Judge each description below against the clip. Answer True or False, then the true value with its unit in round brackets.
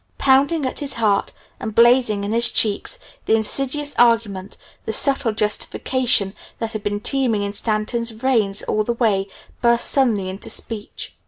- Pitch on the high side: True (225 Hz)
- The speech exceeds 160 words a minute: False (155 wpm)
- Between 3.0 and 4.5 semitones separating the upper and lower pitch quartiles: True (3.5 semitones)